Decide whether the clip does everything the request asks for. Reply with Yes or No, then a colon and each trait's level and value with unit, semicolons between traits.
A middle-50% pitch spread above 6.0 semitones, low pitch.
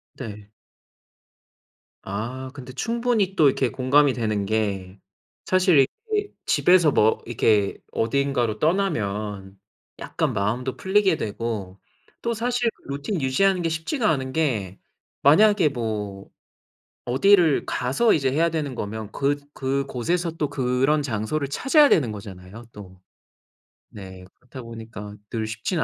Yes: wide, 7.2 semitones; low, 130 Hz